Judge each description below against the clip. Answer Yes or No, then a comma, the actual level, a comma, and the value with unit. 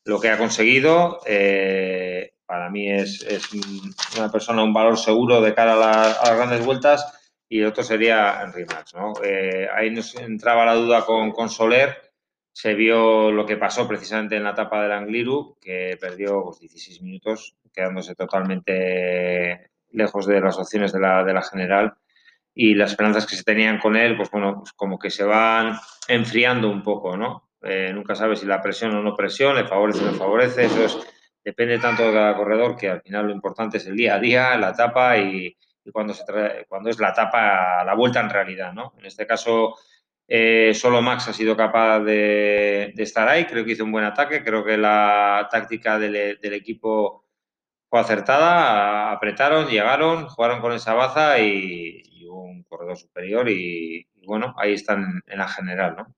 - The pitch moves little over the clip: Yes, narrow, 2.3 semitones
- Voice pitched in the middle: No, low, 110 Hz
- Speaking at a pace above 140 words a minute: Yes, fast, 190 wpm